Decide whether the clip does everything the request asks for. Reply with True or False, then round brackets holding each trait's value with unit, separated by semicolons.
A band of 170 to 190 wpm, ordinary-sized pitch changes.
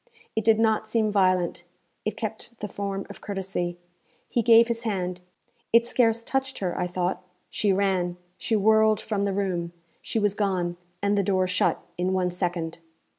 True (175 wpm; 3.1 semitones)